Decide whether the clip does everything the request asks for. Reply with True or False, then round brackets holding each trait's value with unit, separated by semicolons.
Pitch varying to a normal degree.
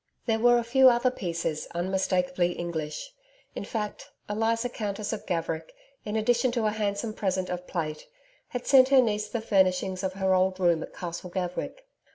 True (4.2 semitones)